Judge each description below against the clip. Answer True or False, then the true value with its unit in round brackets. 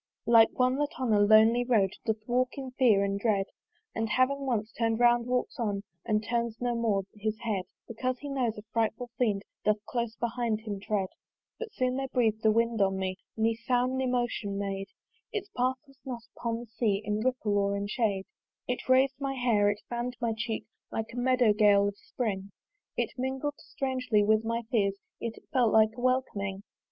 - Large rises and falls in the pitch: False (3.2 semitones)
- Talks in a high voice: True (230 Hz)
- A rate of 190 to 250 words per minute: True (195 wpm)